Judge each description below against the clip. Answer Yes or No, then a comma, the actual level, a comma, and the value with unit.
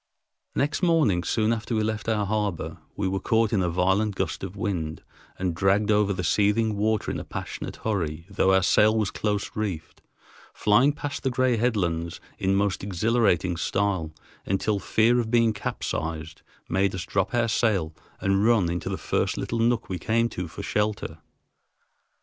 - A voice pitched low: Yes, low, 100 Hz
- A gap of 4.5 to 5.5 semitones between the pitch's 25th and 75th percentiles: No, average, 3.1 semitones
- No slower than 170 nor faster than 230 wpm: Yes, average, 175 wpm